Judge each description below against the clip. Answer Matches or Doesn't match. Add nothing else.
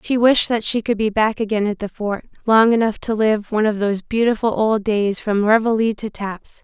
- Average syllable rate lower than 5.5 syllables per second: Matches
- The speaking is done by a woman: Matches